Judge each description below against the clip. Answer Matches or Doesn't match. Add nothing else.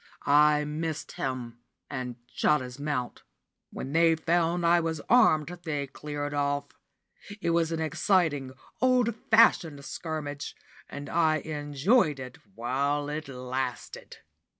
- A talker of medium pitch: Matches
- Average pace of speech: Doesn't match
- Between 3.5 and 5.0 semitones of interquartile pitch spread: Doesn't match